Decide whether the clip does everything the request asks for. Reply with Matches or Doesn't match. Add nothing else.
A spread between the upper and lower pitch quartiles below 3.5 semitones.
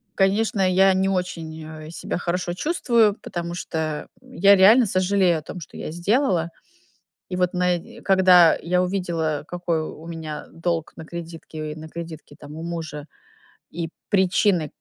Matches